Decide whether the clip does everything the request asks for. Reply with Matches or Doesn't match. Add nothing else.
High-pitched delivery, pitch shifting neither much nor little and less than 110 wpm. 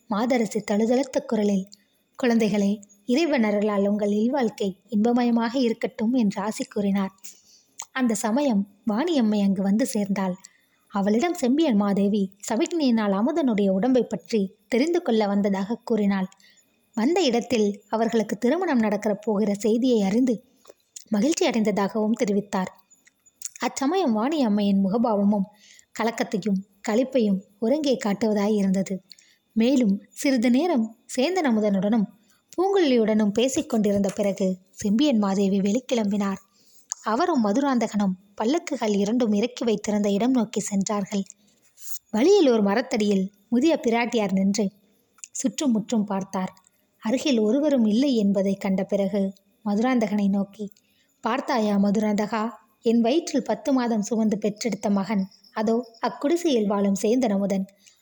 Matches